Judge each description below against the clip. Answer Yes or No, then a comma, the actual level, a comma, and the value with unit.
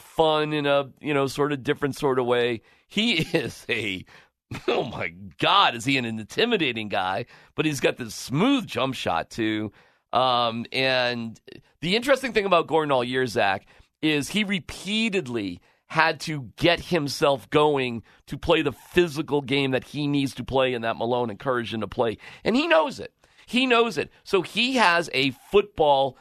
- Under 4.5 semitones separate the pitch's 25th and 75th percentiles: No, wide, 5.4 semitones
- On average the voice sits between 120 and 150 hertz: Yes, medium, 140 Hz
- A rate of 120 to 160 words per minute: No, average, 175 wpm